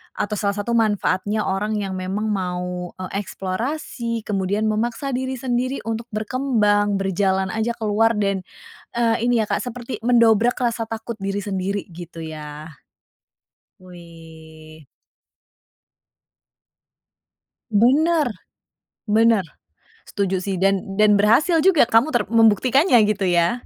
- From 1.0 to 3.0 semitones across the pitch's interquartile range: No, average, 3.7 semitones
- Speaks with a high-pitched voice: Yes, high, 210 Hz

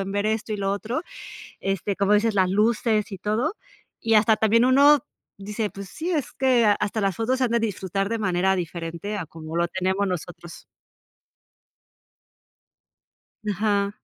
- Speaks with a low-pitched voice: No, high, 205 Hz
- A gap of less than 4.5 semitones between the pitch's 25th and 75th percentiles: Yes, average, 2.9 semitones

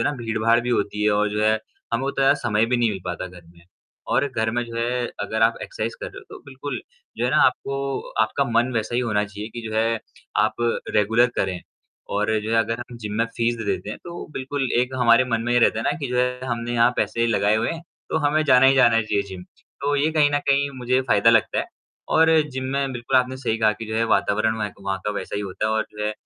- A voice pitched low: Yes, low, 115 Hz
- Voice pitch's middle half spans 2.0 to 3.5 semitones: Yes, average, 2.9 semitones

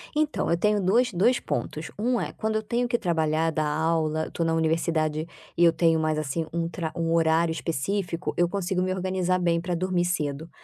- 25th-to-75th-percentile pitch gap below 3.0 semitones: Yes, narrow, 2.6 semitones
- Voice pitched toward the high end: No, medium, 170 Hz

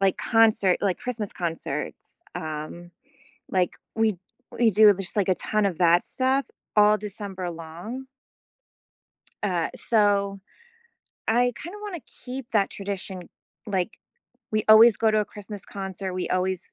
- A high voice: Yes, high, 200 Hz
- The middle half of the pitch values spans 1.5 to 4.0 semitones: Yes, average, 3.2 semitones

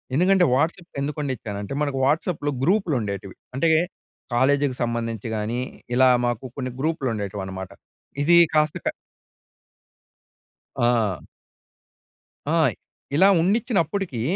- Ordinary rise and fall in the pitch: No, wide, 5.9 semitones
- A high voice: No, low, 135 Hz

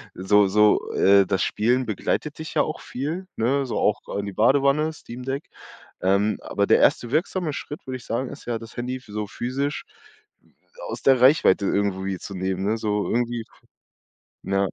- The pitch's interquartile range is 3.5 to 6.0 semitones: Yes, average, 5.1 semitones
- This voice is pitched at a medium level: No, low, 115 Hz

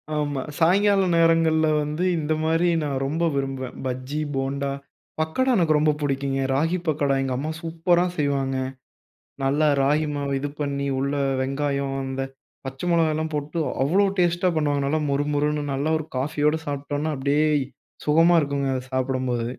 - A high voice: No, medium, 145 Hz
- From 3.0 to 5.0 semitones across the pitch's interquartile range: No, narrow, 2.6 semitones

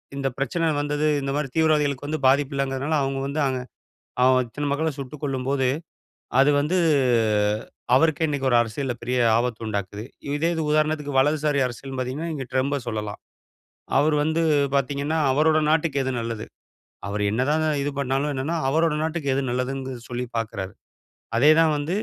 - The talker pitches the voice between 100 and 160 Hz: Yes, medium, 140 Hz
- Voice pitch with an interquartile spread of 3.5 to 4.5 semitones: No, average, 2.9 semitones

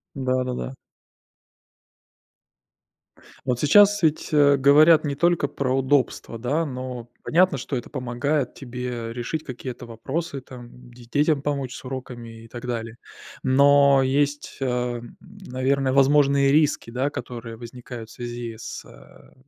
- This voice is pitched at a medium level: No, low, 130 Hz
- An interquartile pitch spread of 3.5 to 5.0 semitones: No, average, 2.8 semitones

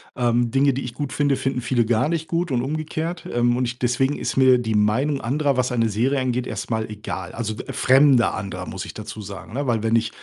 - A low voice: Yes, low, 125 Hz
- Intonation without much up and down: No, average, 3.2 semitones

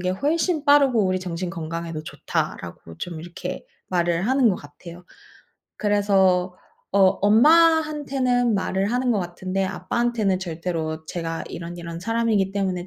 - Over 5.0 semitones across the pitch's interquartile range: Yes, wide, 5.5 semitones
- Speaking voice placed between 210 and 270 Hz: No, high, 190 Hz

